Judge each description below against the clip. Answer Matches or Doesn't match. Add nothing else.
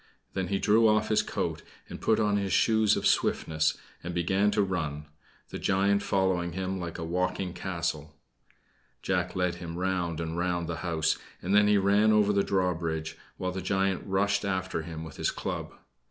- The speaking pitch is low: Matches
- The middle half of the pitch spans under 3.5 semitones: Matches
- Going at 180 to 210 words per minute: Matches